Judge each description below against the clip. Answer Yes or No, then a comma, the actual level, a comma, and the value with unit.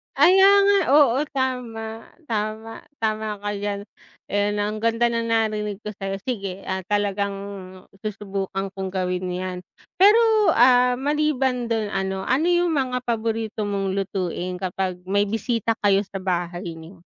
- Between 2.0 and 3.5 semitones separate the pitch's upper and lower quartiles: No, average, 4.0 semitones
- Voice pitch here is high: Yes, high, 210 Hz